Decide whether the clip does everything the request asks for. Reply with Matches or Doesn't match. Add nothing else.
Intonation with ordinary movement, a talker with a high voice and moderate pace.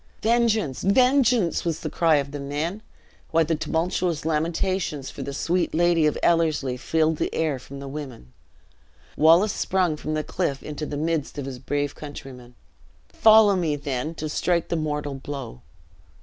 Doesn't match